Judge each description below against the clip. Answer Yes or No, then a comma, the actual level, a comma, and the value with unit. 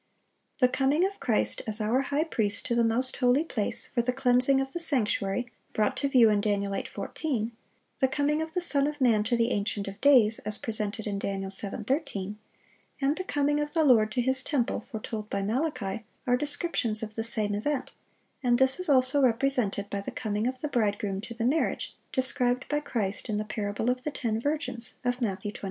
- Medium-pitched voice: No, high, 245 Hz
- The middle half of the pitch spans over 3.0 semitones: Yes, average, 4.4 semitones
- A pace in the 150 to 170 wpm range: No, fast, 205 wpm